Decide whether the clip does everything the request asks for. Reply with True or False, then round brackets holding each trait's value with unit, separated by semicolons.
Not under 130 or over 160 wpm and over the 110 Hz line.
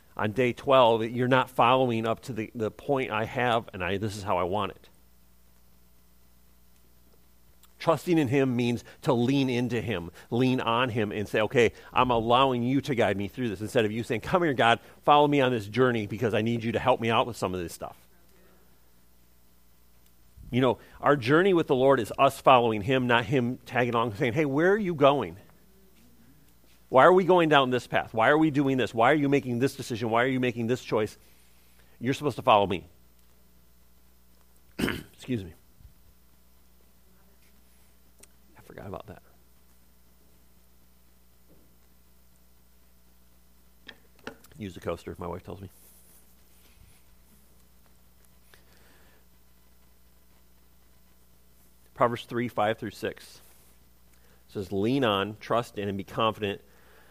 False (155 wpm; 95 Hz)